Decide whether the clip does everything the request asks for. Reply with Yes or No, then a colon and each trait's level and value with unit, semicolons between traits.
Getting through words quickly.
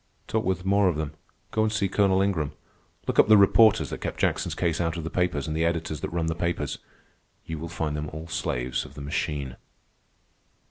Yes: fast, 215 wpm